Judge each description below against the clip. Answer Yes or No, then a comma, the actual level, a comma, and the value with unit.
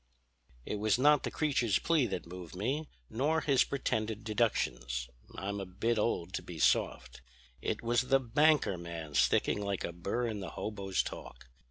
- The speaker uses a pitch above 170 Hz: No, low, 105 Hz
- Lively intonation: Yes, wide, 5.8 semitones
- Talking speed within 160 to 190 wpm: Yes, average, 170 wpm